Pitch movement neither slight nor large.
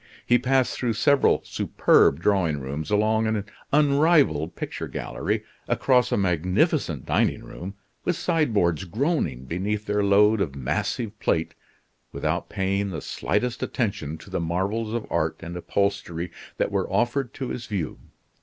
No: wide, 6.1 semitones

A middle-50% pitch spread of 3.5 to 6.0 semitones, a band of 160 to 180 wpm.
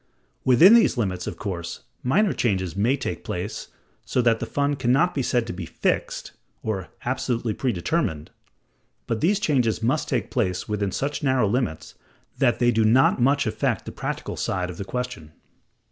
Yes: average, 5.2 semitones; average, 175 wpm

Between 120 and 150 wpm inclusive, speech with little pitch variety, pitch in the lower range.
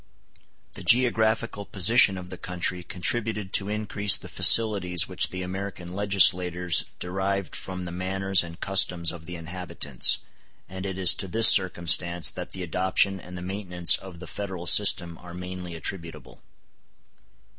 Yes: average, 145 wpm; narrow, 2.0 semitones; very low, 90 Hz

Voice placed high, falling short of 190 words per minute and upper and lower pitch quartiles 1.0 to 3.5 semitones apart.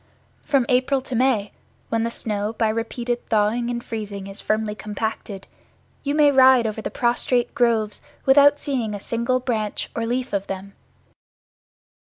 Yes: high, 230 Hz; average, 155 wpm; average, 3.1 semitones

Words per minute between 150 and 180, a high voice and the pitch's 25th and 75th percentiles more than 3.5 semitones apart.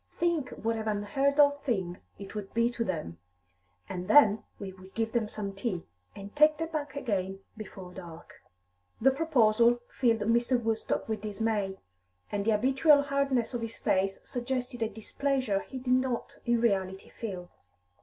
Yes: average, 165 wpm; high, 225 Hz; average, 4.7 semitones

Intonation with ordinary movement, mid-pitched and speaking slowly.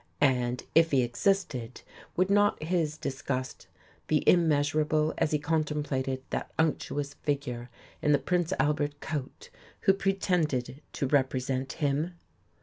Yes: average, 3.6 semitones; medium, 150 Hz; slow, 125 wpm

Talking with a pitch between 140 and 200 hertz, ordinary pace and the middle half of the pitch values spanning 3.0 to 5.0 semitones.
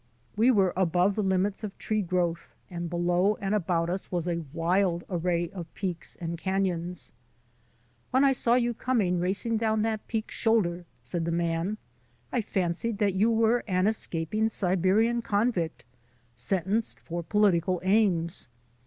Yes: high, 190 Hz; average, 155 wpm; average, 3.9 semitones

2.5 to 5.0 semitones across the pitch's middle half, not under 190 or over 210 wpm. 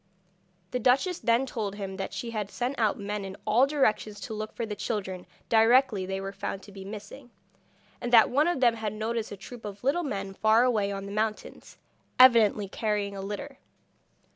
Yes: average, 3.3 semitones; average, 195 wpm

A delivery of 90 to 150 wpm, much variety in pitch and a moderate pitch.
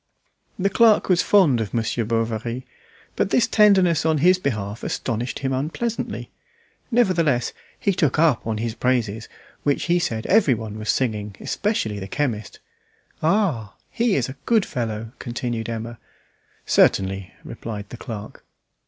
No: average, 140 wpm; wide, 7.7 semitones; low, 125 Hz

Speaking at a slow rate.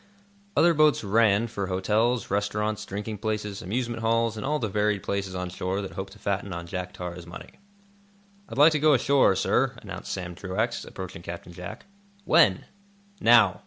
No: average, 170 wpm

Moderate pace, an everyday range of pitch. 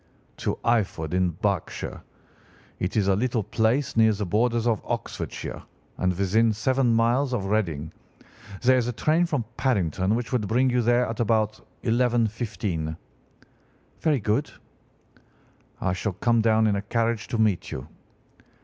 Yes: average, 150 wpm; average, 3.5 semitones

